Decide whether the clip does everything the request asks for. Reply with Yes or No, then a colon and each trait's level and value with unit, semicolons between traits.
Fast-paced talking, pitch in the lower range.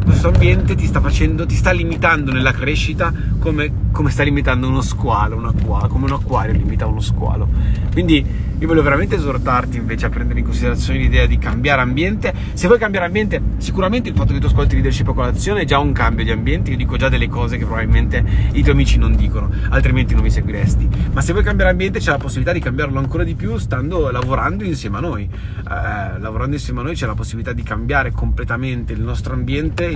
Yes: fast, 210 wpm; low, 110 Hz